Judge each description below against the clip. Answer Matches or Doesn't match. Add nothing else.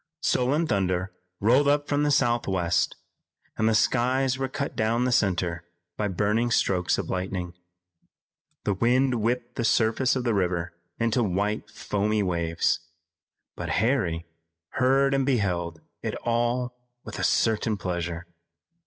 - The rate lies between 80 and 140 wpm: Matches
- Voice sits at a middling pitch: Doesn't match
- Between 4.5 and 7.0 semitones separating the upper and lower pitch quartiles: Matches